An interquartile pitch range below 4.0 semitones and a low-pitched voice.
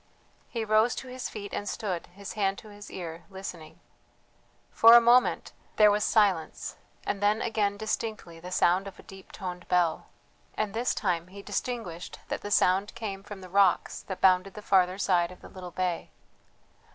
No: average, 2.9 semitones; high, 195 Hz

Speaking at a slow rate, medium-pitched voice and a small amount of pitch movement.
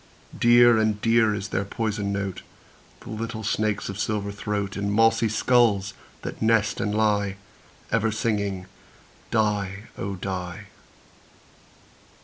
No: slow, 125 wpm; low, 105 Hz; narrow, 2.0 semitones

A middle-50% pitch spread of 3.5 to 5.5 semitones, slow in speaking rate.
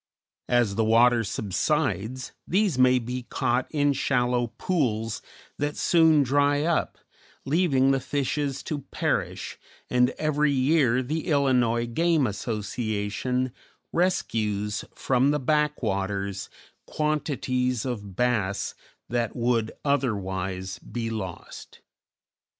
Yes: average, 4.6 semitones; slow, 105 wpm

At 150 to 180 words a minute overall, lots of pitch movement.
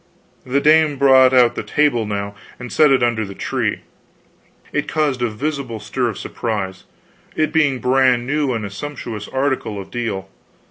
No: average, 170 wpm; average, 4.3 semitones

